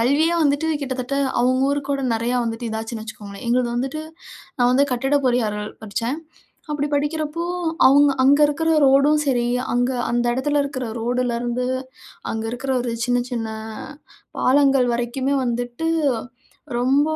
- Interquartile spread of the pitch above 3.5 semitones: No, average, 2.8 semitones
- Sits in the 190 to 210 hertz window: No, very high, 255 Hz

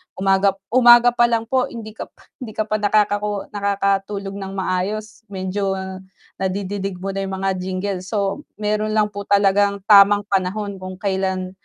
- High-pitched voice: Yes, high, 200 Hz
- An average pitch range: No, narrow, 1.6 semitones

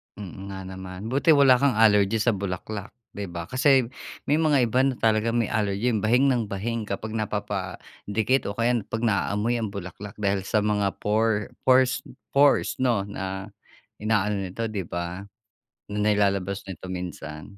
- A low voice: Yes, low, 105 Hz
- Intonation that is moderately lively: Yes, average, 3.1 semitones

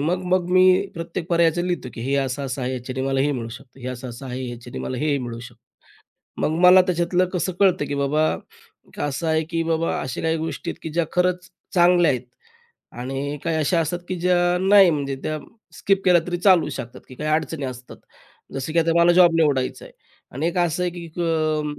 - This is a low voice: No, medium, 160 Hz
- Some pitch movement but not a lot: Yes, average, 4.6 semitones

